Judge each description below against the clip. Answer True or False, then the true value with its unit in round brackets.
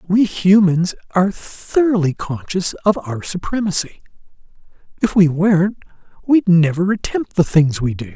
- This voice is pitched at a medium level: True (180 Hz)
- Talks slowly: True (130 wpm)